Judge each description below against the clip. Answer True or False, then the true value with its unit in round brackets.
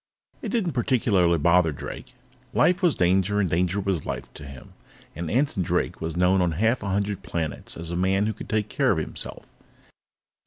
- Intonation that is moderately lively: True (3.8 semitones)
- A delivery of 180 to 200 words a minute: True (190 wpm)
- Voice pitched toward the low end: True (95 Hz)